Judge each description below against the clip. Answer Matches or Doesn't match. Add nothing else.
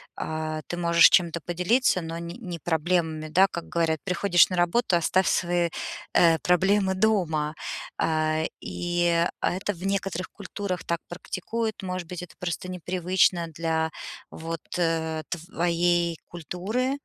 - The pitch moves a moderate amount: Doesn't match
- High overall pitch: Doesn't match